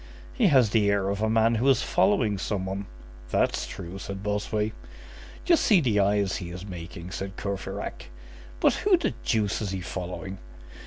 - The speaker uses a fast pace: No, average, 175 wpm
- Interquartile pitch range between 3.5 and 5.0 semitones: No, average, 2.7 semitones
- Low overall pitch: Yes, low, 100 Hz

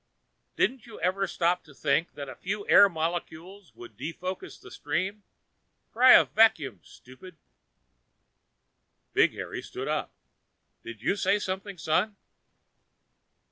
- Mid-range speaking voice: Yes, medium, 180 Hz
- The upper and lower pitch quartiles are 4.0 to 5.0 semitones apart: Yes, average, 4.3 semitones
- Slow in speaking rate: Yes, slow, 125 wpm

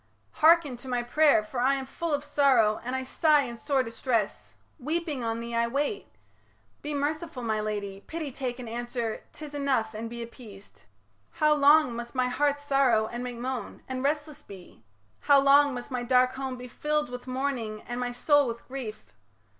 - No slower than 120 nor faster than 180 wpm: No, average, 190 wpm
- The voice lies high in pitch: Yes, very high, 255 Hz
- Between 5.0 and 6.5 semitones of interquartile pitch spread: No, average, 3.6 semitones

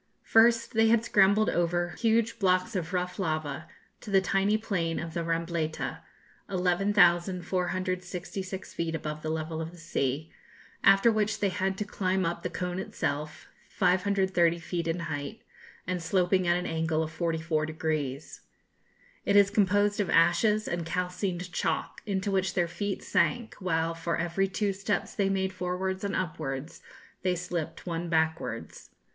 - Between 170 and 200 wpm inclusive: No, average, 150 wpm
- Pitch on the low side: No, medium, 180 Hz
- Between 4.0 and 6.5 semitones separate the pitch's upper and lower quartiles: No, average, 2.8 semitones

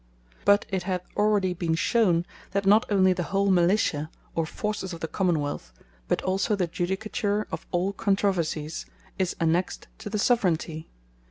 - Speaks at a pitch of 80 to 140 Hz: No, medium, 185 Hz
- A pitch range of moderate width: Yes, average, 3.1 semitones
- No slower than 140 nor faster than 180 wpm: Yes, average, 160 wpm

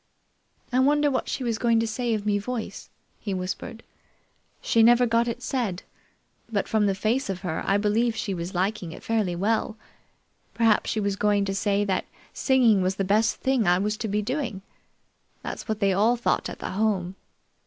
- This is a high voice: Yes, high, 215 Hz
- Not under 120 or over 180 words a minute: No, average, 195 wpm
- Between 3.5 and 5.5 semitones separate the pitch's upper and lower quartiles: No, average, 3.0 semitones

